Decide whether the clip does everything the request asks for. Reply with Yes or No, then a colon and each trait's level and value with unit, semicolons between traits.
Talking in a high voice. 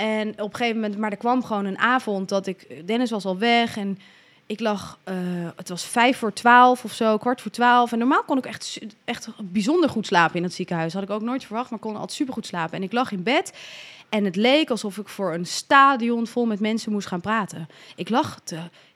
Yes: high, 215 Hz